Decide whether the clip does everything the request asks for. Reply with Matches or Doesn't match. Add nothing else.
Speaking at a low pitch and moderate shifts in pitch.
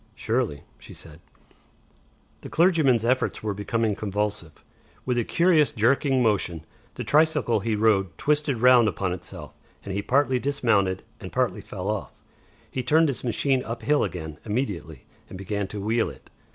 Matches